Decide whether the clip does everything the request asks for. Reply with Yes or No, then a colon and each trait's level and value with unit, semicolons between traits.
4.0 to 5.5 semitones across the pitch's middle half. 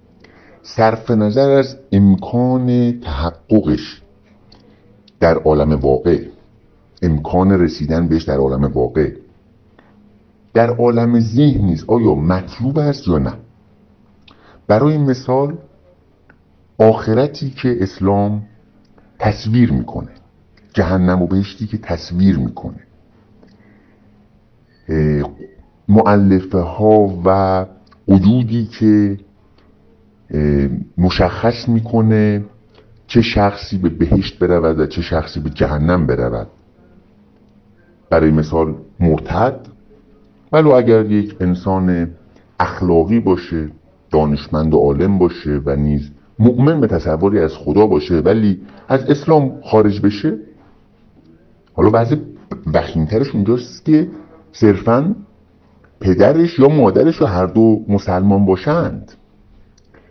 Yes: average, 5.1 semitones